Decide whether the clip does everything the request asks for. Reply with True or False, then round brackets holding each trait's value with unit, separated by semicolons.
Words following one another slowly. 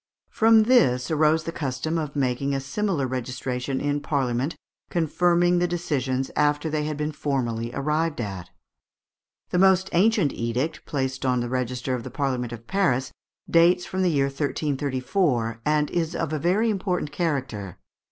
False (155 wpm)